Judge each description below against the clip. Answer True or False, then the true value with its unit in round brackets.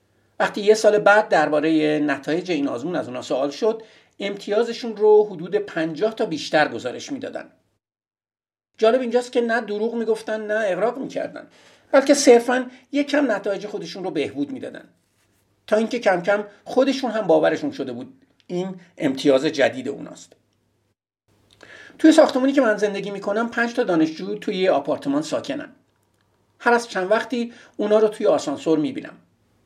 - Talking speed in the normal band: True (145 wpm)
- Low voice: False (215 Hz)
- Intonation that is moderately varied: False (6.3 semitones)